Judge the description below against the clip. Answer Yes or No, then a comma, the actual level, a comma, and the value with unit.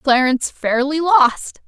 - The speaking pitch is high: Yes, very high, 280 Hz